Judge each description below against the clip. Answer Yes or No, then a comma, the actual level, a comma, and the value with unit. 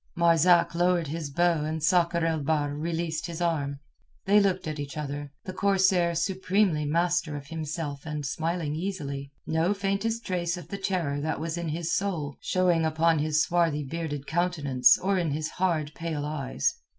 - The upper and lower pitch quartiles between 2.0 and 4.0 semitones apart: Yes, average, 2.9 semitones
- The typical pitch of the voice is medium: Yes, medium, 165 Hz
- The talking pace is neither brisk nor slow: Yes, average, 170 wpm